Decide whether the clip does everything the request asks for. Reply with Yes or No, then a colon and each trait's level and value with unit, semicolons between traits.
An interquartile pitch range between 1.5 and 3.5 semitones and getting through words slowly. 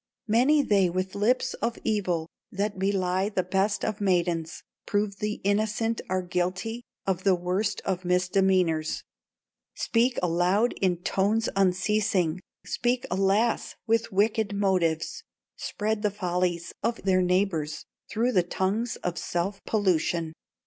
Yes: average, 2.9 semitones; slow, 130 wpm